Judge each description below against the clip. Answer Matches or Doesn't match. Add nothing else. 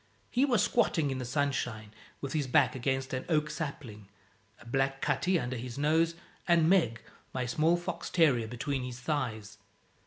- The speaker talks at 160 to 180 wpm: Matches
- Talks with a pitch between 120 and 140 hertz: Matches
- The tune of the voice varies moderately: Matches